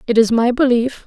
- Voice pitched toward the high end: Yes, high, 240 Hz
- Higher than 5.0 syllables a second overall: Yes, 5.5 syllables/s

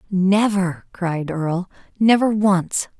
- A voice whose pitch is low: No, high, 190 Hz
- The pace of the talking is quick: No, slow, 100 wpm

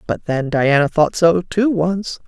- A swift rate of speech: No, average, 185 wpm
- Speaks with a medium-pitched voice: Yes, medium, 170 Hz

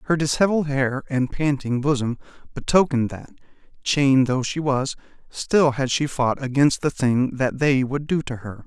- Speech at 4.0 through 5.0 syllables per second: Yes, 4.8 syllables/s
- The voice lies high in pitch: No, low, 135 Hz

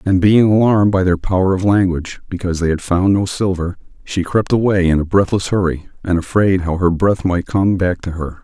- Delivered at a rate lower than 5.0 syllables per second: Yes, 4.8 syllables/s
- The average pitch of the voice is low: Yes, very low, 95 Hz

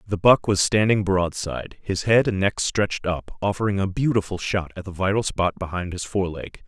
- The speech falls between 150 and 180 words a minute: No, fast, 205 wpm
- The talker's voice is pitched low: Yes, very low, 95 Hz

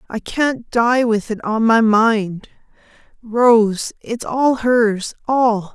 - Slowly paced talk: Yes, slow, 115 wpm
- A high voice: Yes, high, 225 Hz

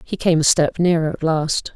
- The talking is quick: Yes, fast, 240 wpm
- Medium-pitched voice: Yes, medium, 165 Hz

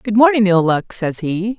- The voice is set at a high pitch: Yes, high, 205 Hz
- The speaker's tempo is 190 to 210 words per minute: No, fast, 225 wpm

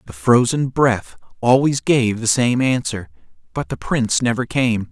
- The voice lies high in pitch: No, low, 115 Hz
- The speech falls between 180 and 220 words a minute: No, average, 160 wpm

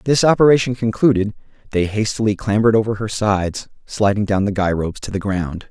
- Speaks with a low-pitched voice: Yes, low, 105 Hz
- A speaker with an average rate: Yes, average, 180 wpm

